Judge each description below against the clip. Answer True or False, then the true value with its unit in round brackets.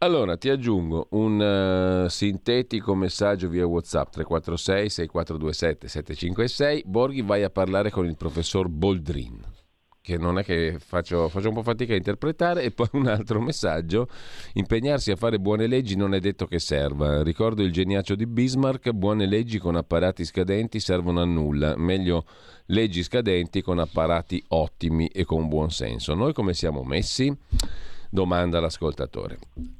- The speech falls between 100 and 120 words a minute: False (145 wpm)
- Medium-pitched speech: False (95 Hz)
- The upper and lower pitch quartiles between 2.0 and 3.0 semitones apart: False (4.4 semitones)